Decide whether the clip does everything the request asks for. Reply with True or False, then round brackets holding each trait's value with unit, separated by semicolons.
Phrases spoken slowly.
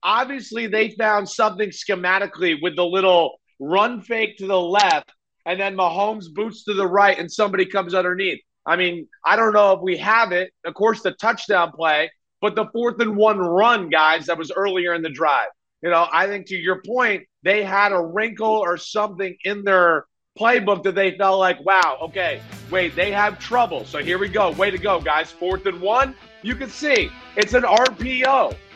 False (195 wpm)